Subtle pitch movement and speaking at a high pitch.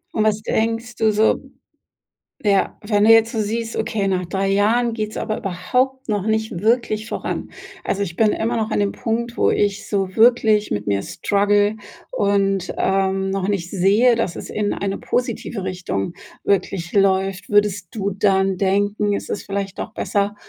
Yes: narrow, 2.1 semitones; high, 205 Hz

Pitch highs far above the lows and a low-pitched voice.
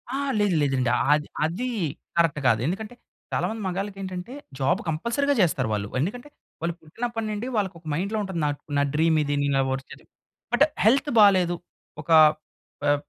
No: wide, 6.4 semitones; medium, 180 Hz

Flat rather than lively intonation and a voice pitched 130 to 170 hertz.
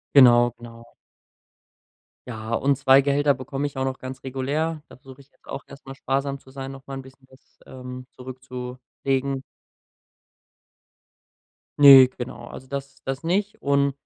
Yes: narrow, 1.4 semitones; low, 135 Hz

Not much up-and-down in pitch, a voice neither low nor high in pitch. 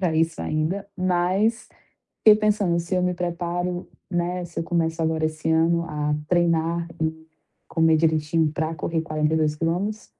Yes: narrow, 1.9 semitones; medium, 165 Hz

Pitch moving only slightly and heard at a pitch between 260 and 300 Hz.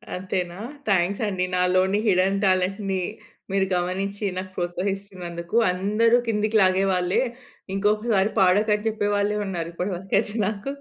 No: narrow, 2.2 semitones; high, 195 Hz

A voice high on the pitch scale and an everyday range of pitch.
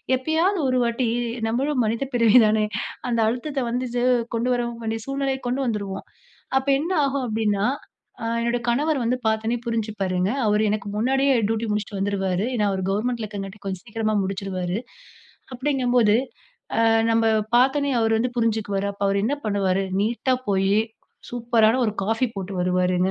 Yes: high, 225 Hz; average, 3.7 semitones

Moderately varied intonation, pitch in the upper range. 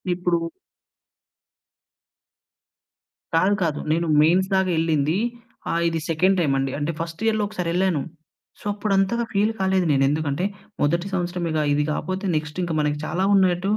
No: average, 3.4 semitones; medium, 175 Hz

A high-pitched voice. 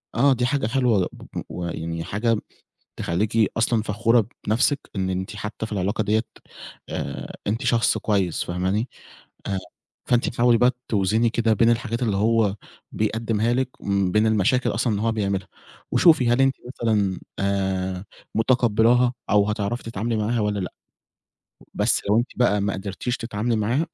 No: low, 110 Hz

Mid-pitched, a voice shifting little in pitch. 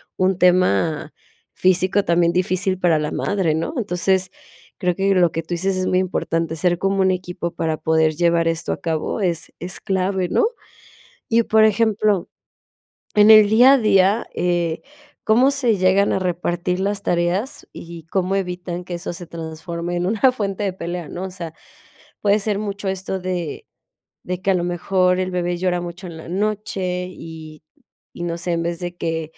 Yes: medium, 180 Hz; narrow, 2.3 semitones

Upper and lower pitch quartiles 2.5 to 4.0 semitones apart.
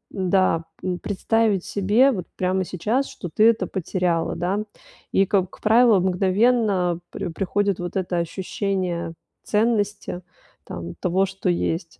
Yes: average, 2.8 semitones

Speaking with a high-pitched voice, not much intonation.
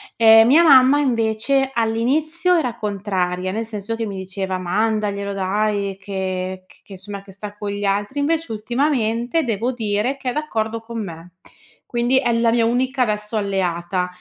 No: high, 220 Hz; average, 3.7 semitones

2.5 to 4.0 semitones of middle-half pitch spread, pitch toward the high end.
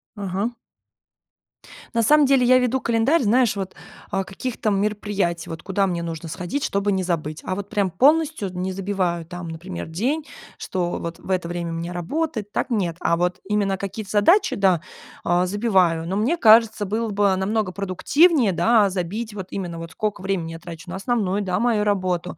Yes: average, 3.7 semitones; high, 195 Hz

